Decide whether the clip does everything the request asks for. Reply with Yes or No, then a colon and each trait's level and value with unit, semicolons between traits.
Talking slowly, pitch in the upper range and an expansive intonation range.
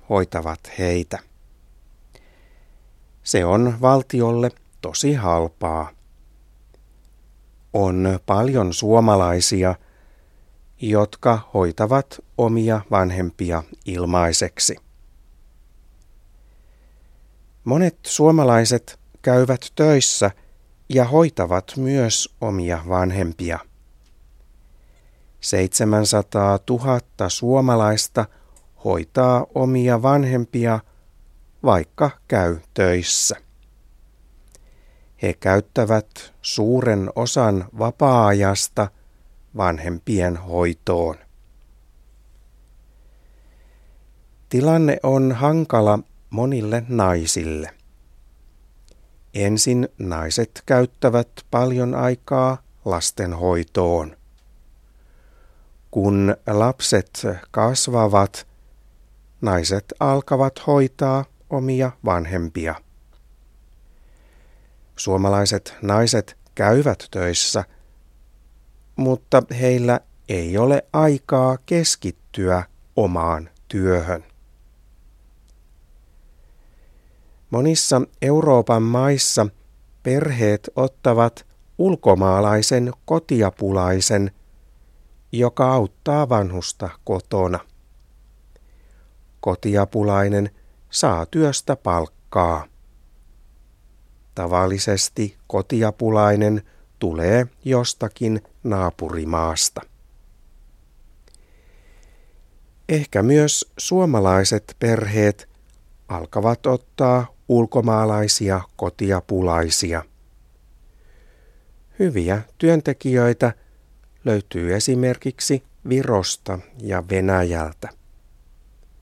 No: slow, 55 wpm; low, 100 Hz; wide, 6.2 semitones